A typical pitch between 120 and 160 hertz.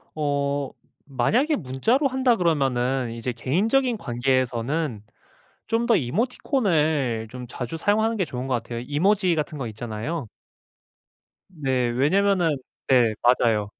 Yes: medium, 140 Hz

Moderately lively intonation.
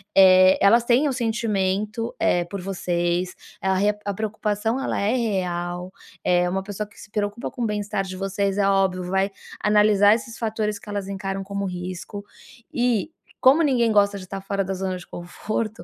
No: narrow, 2.3 semitones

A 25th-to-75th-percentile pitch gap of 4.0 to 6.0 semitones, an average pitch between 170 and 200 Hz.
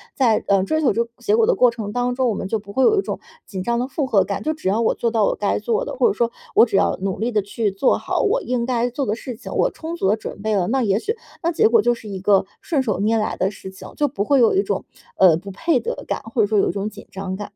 No: average, 5.2 semitones; high, 230 Hz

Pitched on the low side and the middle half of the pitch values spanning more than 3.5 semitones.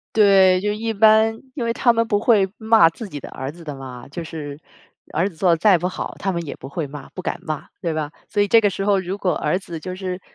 No: medium, 185 Hz; average, 4.7 semitones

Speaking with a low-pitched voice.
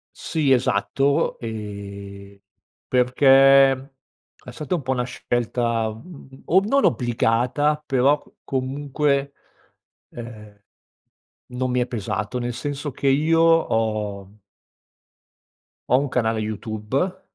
Yes: low, 125 Hz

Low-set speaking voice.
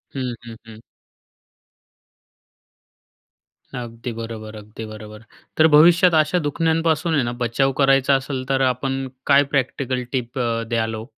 Yes: low, 130 Hz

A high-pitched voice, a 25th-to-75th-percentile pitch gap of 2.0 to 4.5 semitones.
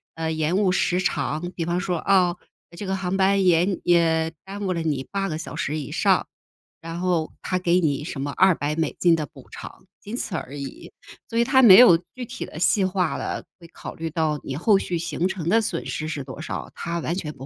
No: medium, 170 Hz; average, 3.1 semitones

